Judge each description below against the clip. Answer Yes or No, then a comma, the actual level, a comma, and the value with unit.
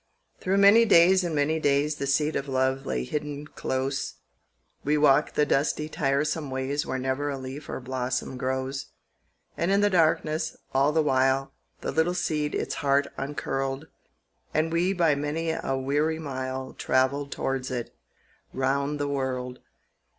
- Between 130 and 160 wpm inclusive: Yes, average, 155 wpm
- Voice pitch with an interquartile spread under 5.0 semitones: Yes, average, 2.8 semitones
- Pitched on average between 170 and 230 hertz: No, medium, 140 Hz